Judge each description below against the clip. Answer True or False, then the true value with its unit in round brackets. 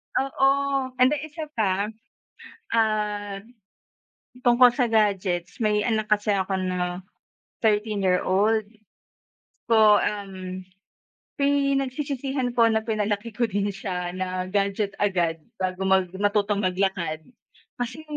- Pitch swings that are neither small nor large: True (3.3 semitones)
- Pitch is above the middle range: True (205 Hz)